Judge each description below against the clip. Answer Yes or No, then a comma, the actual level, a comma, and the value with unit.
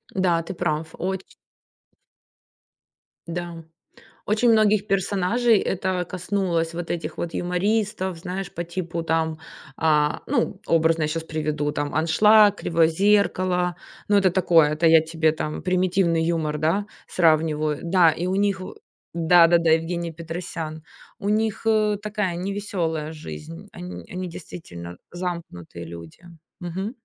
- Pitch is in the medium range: Yes, medium, 170 Hz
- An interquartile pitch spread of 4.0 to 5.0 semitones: No, average, 3.0 semitones